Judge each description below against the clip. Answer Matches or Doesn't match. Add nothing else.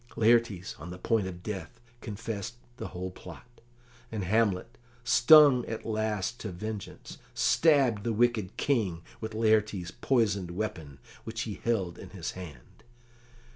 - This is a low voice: Matches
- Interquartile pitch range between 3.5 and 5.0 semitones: Matches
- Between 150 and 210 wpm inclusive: Doesn't match